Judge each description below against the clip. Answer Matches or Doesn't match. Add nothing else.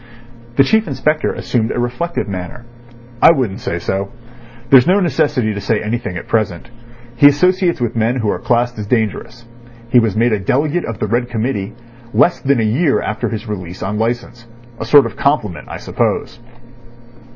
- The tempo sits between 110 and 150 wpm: Doesn't match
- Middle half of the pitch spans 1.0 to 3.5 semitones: Doesn't match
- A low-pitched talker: Matches